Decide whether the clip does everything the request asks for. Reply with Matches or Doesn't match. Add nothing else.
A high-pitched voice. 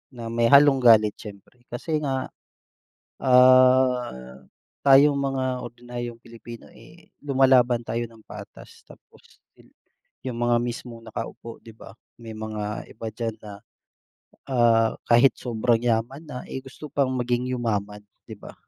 Doesn't match